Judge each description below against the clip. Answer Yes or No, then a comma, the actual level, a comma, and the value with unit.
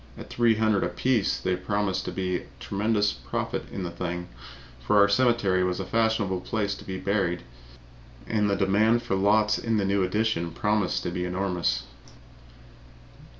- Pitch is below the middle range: Yes, low, 100 Hz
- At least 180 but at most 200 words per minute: No, average, 170 wpm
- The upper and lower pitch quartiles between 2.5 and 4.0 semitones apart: Yes, average, 2.8 semitones